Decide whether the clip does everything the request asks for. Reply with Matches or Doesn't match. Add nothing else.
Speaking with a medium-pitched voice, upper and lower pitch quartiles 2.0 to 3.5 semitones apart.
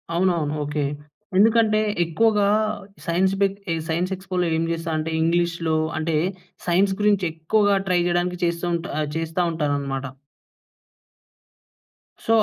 Matches